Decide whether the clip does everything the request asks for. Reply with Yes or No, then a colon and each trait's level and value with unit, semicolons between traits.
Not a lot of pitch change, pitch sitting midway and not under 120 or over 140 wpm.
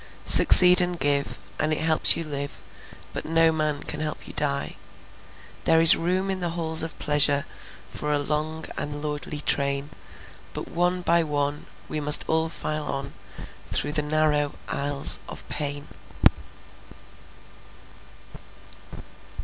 Yes: narrow, 2.0 semitones; medium, 150 Hz; slow, 135 wpm